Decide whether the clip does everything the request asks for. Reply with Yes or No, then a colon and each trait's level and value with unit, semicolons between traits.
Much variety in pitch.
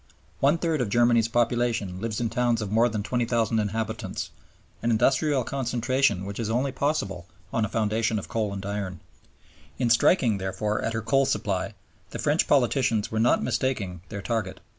No: average, 2.9 semitones